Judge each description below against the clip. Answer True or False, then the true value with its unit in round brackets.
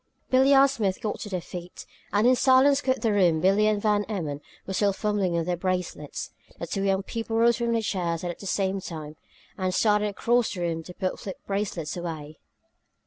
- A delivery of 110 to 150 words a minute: False (205 wpm)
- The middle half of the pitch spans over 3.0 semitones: True (4.0 semitones)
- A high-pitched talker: True (195 Hz)